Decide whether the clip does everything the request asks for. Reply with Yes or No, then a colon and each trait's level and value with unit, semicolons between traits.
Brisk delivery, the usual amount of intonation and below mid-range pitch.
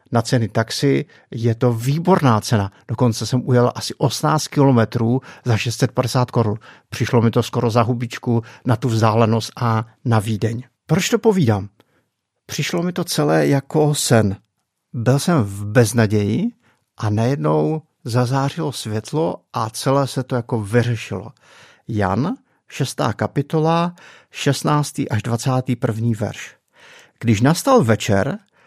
No: average, 130 wpm; average, 3.6 semitones; low, 120 Hz